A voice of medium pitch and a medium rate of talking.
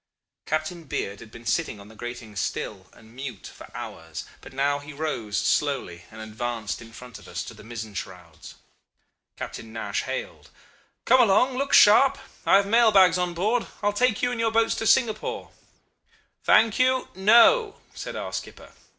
Yes: medium, 155 Hz; average, 175 wpm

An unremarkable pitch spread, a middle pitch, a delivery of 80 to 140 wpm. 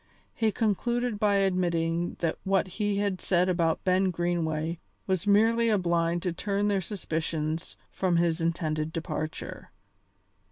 Yes: average, 3.4 semitones; medium, 180 Hz; slow, 135 wpm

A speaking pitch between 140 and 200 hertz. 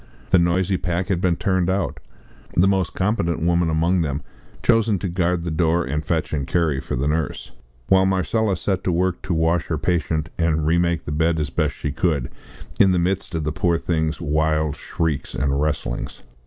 No: very low, 85 Hz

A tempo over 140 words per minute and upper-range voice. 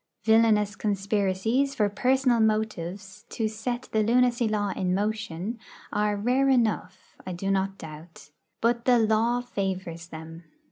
No: slow, 135 wpm; high, 210 Hz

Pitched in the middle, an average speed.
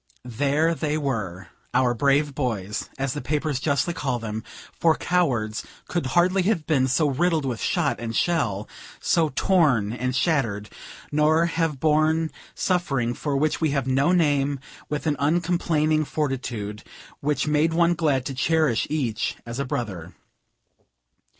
Yes: medium, 145 Hz; average, 145 wpm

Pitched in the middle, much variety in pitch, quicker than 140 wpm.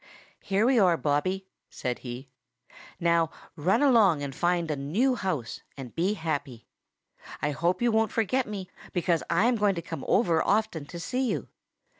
Yes: medium, 175 Hz; wide, 5.7 semitones; average, 170 wpm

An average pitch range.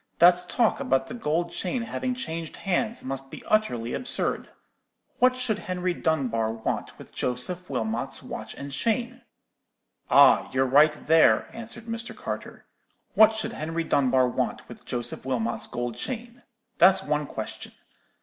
No: wide, 9.0 semitones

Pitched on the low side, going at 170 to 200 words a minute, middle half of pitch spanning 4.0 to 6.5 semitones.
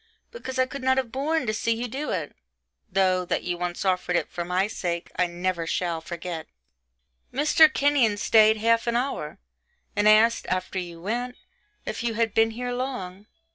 No: high, 215 Hz; average, 180 wpm; wide, 5.5 semitones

